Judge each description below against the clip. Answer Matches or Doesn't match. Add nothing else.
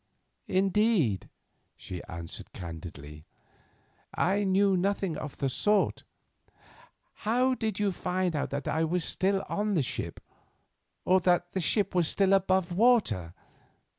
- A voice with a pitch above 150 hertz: Matches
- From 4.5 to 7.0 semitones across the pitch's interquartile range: Matches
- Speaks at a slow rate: Matches